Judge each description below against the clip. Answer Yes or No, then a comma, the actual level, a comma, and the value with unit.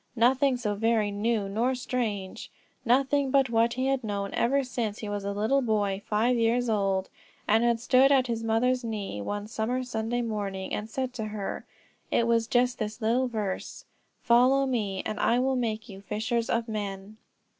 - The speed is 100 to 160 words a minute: No, average, 185 wpm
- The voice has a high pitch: Yes, high, 225 Hz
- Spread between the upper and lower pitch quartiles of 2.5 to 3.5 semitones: Yes, average, 3.0 semitones